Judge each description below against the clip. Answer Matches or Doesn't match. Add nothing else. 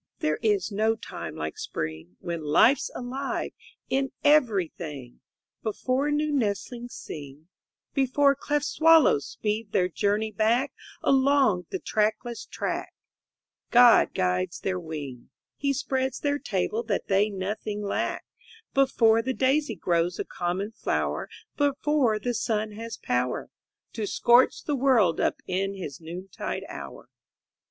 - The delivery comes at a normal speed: Doesn't match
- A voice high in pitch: Matches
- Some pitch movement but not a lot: Doesn't match